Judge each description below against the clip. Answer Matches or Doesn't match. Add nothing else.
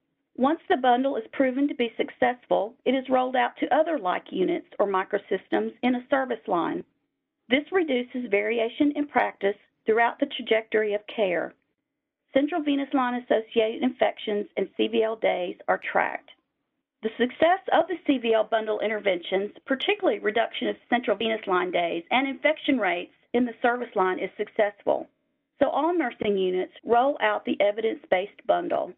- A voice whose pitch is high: Matches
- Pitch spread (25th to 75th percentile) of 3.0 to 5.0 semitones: Doesn't match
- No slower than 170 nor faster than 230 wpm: Doesn't match